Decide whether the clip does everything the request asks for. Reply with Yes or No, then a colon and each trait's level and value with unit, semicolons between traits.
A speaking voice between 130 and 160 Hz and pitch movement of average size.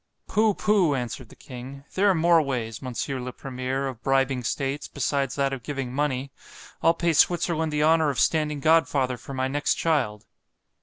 Yes: medium, 140 Hz; average, 3.5 semitones